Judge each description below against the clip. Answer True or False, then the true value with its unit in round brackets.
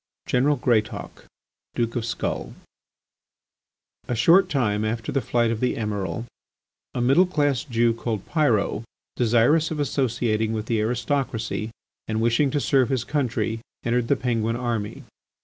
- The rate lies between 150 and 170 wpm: False (140 wpm)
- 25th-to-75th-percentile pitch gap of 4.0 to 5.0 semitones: False (3.2 semitones)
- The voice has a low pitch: True (120 Hz)